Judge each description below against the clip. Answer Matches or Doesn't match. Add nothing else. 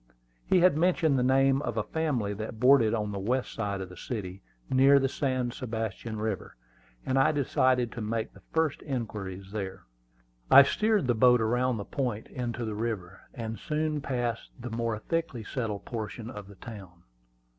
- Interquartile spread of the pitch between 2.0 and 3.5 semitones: Doesn't match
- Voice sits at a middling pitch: Doesn't match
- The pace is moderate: Matches